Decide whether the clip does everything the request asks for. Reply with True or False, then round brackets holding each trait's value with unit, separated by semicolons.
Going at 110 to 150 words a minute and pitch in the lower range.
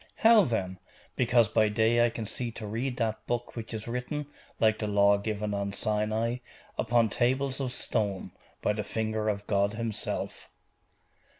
False (165 wpm; 110 Hz)